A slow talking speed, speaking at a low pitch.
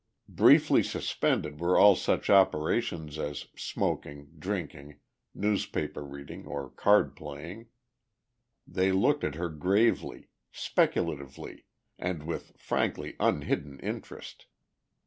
Yes: slow, 100 wpm; very low, 80 Hz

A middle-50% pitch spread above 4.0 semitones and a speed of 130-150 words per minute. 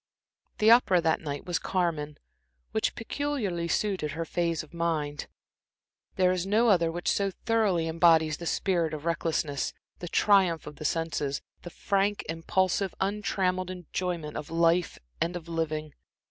No: average, 2.8 semitones; average, 145 wpm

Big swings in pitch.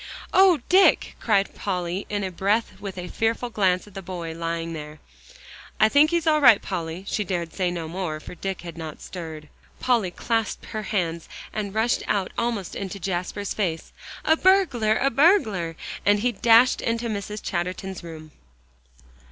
No: average, 4.8 semitones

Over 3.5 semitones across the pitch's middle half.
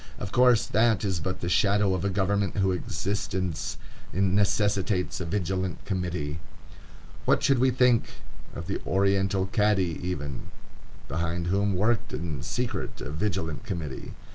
No: average, 2.8 semitones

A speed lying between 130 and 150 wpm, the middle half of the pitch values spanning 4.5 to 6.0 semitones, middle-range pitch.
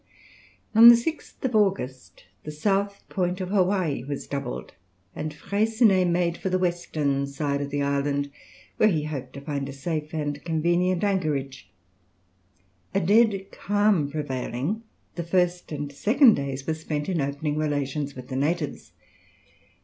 Yes: average, 145 wpm; average, 5.1 semitones; medium, 155 Hz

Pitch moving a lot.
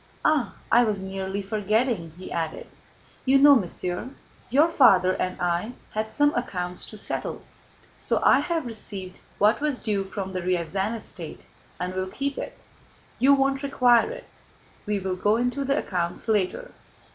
Yes: wide, 5.9 semitones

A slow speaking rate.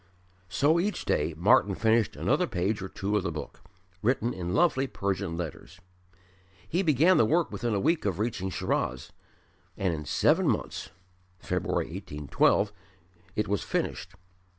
No: average, 150 wpm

